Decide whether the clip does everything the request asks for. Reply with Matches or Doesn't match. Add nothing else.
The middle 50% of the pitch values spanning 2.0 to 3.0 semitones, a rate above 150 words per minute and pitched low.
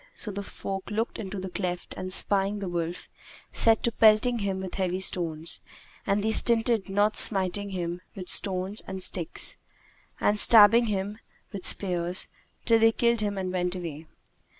Doesn't match